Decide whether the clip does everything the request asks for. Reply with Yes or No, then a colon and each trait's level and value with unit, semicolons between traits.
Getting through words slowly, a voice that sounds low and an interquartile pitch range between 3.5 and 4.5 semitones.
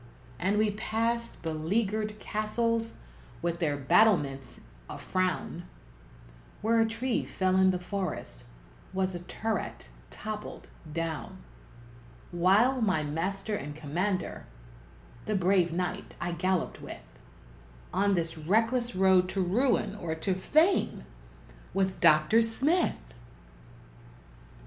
No: slow, 110 wpm; high, 190 Hz; average, 4.2 semitones